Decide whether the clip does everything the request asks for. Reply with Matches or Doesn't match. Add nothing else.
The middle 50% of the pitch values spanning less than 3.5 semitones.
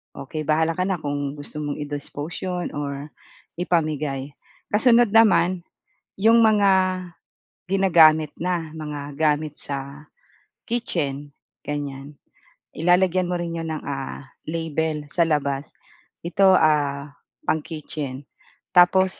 Doesn't match